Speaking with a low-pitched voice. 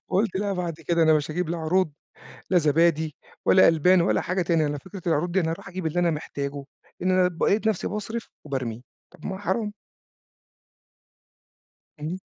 No: medium, 170 Hz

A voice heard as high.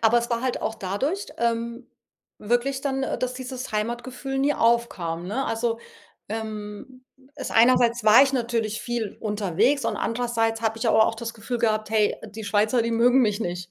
Yes: high, 230 Hz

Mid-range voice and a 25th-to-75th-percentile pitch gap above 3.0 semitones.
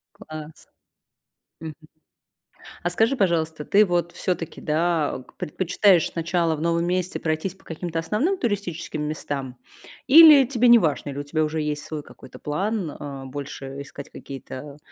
Yes: medium, 165 Hz; average, 4.0 semitones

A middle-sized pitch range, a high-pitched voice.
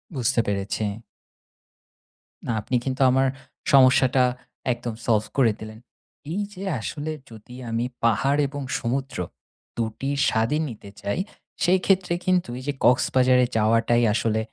No: average, 3.5 semitones; low, 125 Hz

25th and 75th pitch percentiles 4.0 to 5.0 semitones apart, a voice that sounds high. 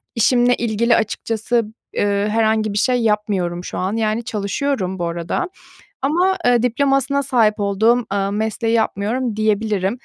No: average, 3.2 semitones; high, 220 Hz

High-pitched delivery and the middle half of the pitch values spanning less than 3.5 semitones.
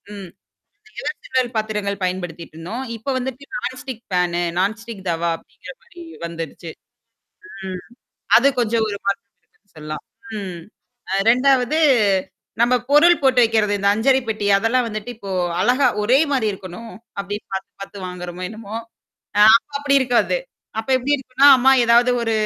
No: high, 220 Hz; average, 4.8 semitones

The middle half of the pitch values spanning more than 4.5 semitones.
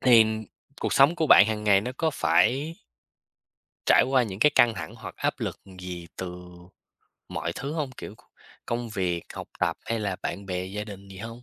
Yes: average, 4.9 semitones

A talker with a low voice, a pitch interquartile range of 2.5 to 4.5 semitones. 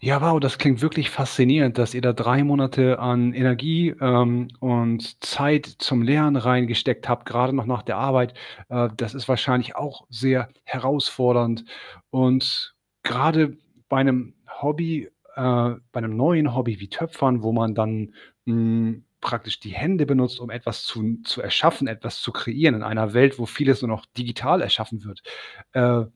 Yes: low, 125 Hz; average, 2.8 semitones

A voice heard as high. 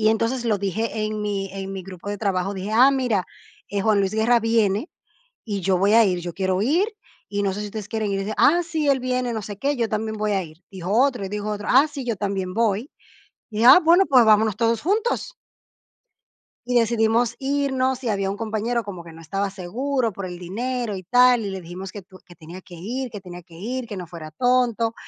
Yes: high, 215 Hz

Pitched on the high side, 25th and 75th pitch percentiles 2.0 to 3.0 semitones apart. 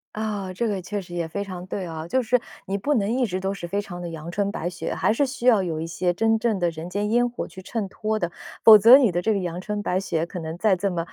No: high, 195 Hz; average, 3.7 semitones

